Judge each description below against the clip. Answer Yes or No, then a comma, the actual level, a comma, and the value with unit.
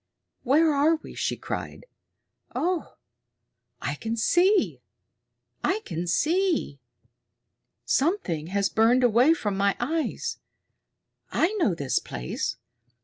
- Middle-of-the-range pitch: No, very high, 255 Hz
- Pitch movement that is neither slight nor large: No, wide, 8.8 semitones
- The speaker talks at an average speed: No, slow, 105 wpm